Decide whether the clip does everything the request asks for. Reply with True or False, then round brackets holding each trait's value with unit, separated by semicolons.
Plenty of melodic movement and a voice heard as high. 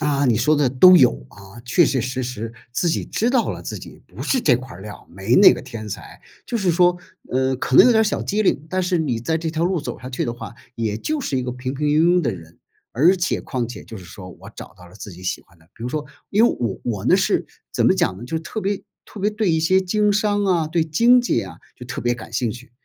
False (7.6 semitones; 135 Hz)